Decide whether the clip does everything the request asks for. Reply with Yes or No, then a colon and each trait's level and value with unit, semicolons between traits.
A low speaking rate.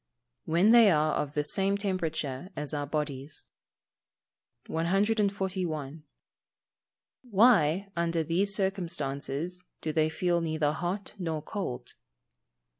Yes: slow, 110 wpm